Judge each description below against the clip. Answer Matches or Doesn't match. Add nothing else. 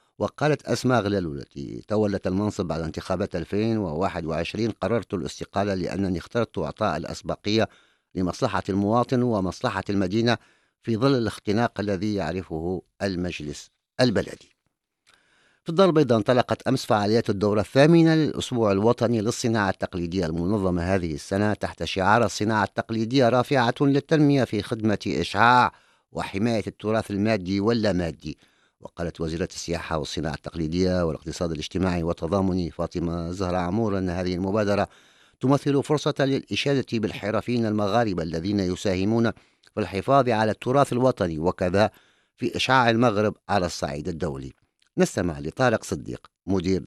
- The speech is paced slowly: Matches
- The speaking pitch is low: Matches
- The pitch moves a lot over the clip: Doesn't match